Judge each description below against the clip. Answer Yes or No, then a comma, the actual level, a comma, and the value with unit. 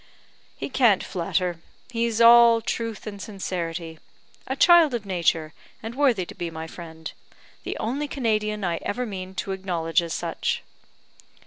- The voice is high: Yes, high, 200 Hz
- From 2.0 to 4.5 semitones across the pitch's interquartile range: No, average, 5.3 semitones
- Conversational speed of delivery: Yes, average, 145 wpm